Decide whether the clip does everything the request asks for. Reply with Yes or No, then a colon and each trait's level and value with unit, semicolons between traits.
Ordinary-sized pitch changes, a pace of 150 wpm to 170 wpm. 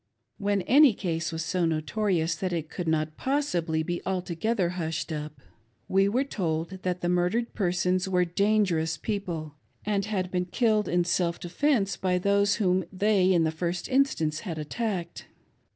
Yes: average, 3.4 semitones; average, 165 wpm